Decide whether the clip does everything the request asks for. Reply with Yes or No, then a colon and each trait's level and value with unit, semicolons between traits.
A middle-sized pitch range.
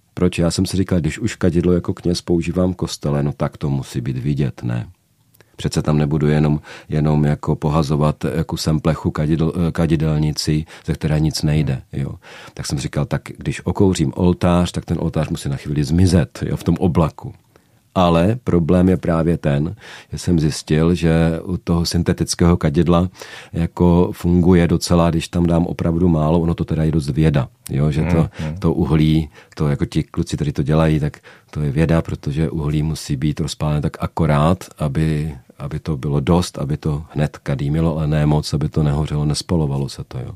No: narrow, 2.3 semitones